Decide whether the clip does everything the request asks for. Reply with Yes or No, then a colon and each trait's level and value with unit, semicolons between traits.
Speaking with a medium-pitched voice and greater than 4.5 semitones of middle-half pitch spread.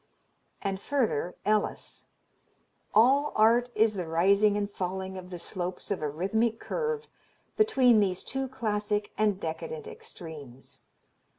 No: high, 210 Hz; average, 5.1 semitones